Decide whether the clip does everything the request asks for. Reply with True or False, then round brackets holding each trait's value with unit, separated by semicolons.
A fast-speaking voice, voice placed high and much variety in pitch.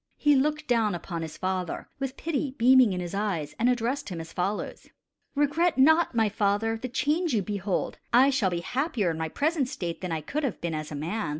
True (215 wpm; 220 Hz; 7.3 semitones)